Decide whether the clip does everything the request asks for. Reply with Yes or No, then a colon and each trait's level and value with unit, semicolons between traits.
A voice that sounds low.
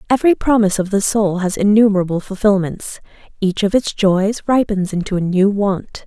No: high, 200 Hz